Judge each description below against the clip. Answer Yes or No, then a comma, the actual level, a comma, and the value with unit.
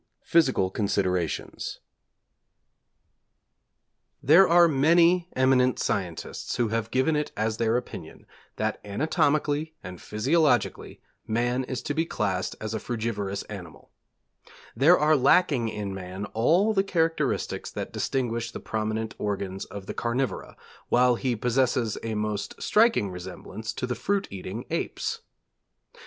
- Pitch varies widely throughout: Yes, wide, 6.0 semitones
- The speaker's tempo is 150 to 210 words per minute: No, slow, 135 wpm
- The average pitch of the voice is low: Yes, low, 120 Hz